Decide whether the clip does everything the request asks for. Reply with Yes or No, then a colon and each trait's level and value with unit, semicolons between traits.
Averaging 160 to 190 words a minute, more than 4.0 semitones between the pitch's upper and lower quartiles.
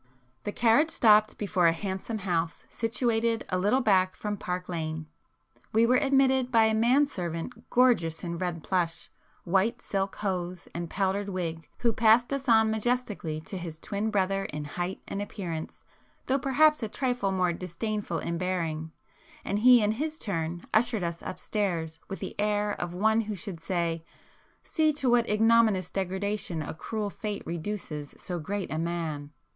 Yes: average, 165 wpm; average, 4.7 semitones